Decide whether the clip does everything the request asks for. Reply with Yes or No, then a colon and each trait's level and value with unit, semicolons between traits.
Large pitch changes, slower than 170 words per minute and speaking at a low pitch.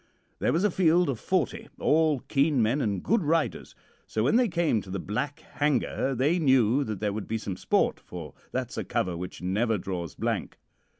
No: wide, 7.4 semitones; average, 195 wpm; low, 130 Hz